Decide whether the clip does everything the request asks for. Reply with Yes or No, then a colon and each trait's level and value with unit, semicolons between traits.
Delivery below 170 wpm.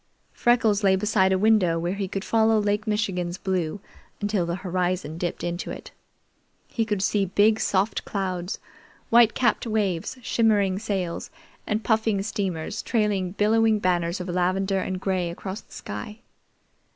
Yes: average, 150 wpm